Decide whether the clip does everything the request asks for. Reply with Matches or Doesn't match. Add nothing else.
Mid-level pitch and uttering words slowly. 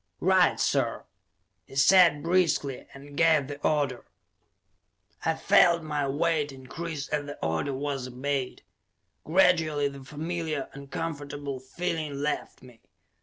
Matches